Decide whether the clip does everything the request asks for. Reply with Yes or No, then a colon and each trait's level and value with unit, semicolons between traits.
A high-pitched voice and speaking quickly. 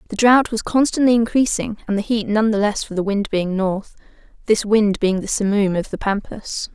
Yes: high, 210 Hz; fast, 215 wpm